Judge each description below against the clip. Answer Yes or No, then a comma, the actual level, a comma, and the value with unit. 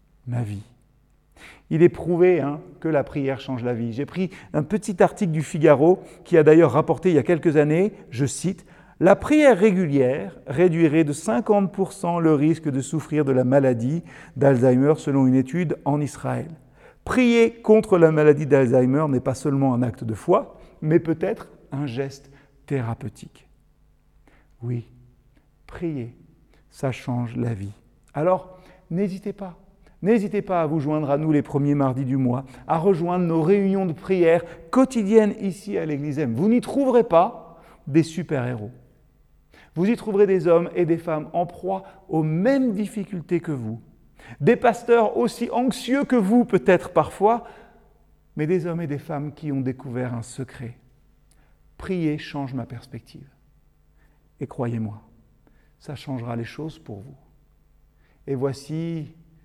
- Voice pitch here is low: No, medium, 155 Hz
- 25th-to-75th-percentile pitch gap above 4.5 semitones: Yes, average, 5.3 semitones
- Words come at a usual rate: Yes, average, 155 wpm